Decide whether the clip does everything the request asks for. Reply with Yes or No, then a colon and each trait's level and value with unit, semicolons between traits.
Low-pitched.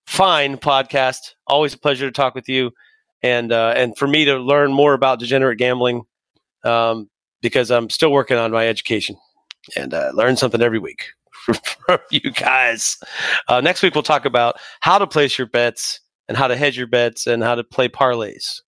Yes: low, 130 Hz